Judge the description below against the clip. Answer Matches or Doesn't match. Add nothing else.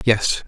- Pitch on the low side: Matches